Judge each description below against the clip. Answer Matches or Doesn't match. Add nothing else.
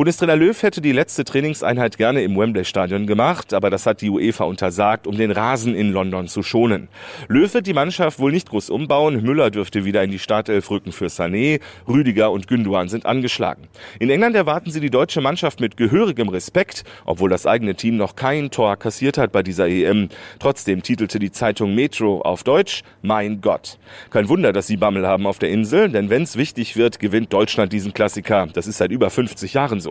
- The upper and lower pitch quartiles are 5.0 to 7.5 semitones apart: Matches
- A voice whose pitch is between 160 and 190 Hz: Doesn't match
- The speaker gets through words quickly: Matches